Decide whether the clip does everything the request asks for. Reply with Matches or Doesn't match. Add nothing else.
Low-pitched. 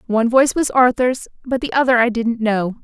Doesn't match